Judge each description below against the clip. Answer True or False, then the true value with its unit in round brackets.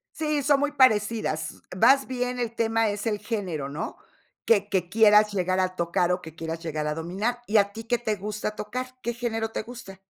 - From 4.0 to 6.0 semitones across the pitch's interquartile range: True (4.3 semitones)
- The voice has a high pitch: True (210 Hz)